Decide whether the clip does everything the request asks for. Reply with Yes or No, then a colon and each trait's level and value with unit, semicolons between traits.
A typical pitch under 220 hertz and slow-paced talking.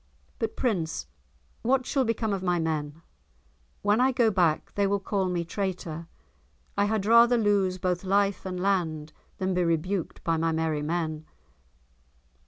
No: medium, 185 Hz; average, 155 wpm